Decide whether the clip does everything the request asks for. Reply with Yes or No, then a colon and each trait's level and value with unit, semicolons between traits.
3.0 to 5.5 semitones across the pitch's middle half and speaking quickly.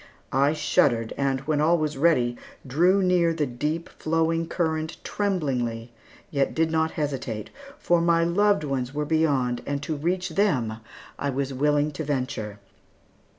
No: average, 3.7 semitones; average, 150 wpm